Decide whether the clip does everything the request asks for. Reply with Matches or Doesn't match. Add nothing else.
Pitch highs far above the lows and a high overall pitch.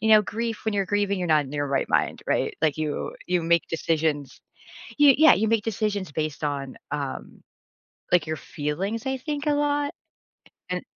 Doesn't match